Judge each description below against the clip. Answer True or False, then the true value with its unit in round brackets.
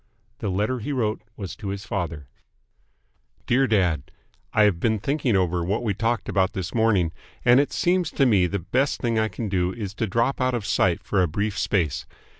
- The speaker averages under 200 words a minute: False (205 wpm)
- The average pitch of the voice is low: True (105 Hz)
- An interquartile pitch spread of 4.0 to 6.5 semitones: True (4.3 semitones)